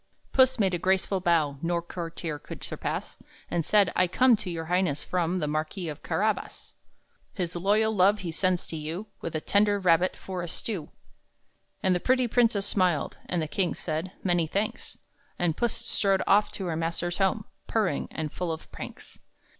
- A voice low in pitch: No, medium, 180 Hz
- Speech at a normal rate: Yes, average, 180 wpm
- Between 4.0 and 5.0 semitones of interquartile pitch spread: No, average, 3.3 semitones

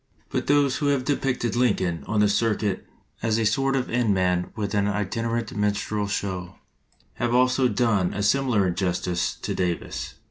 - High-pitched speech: No, low, 105 Hz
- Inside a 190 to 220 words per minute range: No, average, 165 wpm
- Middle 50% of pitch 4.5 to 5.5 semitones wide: No, average, 4.1 semitones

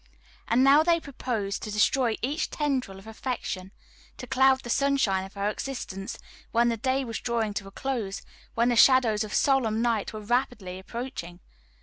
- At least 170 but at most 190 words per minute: Yes, average, 175 wpm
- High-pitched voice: Yes, high, 235 Hz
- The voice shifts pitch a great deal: No, average, 4.3 semitones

